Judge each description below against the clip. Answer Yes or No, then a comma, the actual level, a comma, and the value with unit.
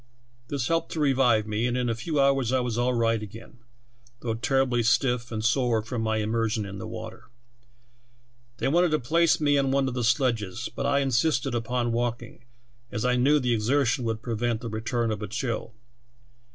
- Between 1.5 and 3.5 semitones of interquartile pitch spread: Yes, average, 2.9 semitones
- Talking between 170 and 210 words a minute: Yes, average, 190 wpm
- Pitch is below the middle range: Yes, low, 120 Hz